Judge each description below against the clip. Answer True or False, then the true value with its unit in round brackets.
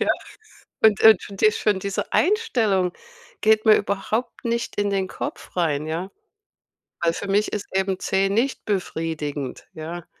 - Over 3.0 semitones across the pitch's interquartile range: True (3.7 semitones)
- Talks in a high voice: True (195 Hz)